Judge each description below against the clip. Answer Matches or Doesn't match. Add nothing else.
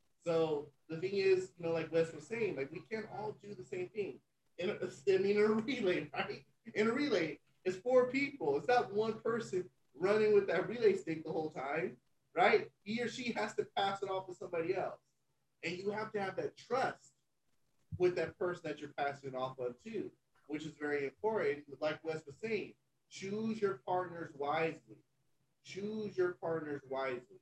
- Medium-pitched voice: Matches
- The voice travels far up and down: Matches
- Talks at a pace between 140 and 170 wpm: Doesn't match